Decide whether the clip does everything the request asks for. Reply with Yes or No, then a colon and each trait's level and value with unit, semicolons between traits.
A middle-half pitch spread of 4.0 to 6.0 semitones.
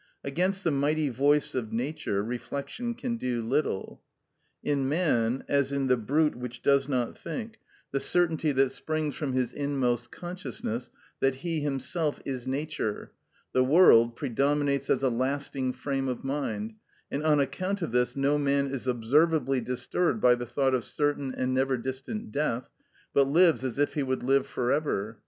No: average, 2.9 semitones